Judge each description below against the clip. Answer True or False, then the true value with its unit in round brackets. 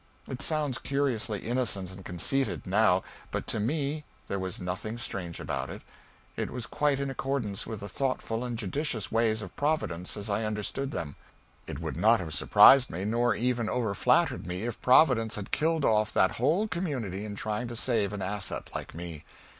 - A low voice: True (110 Hz)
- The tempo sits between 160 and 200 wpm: True (185 wpm)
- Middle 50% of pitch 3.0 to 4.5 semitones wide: False (5.1 semitones)